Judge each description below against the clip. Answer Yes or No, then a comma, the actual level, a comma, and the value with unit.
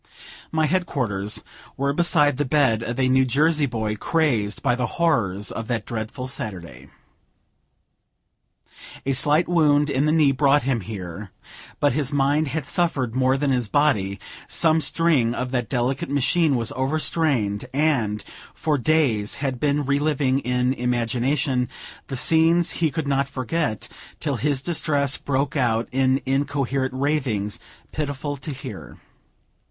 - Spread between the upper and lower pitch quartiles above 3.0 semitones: Yes, average, 3.6 semitones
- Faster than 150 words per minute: No, average, 145 wpm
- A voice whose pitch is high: No, low, 135 Hz